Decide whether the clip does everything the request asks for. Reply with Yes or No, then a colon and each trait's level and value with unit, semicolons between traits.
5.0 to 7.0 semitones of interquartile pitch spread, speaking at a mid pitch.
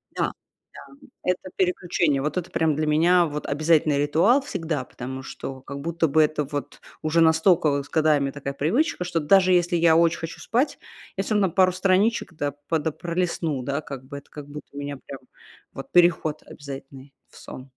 No: average, 3.7 semitones; medium, 155 Hz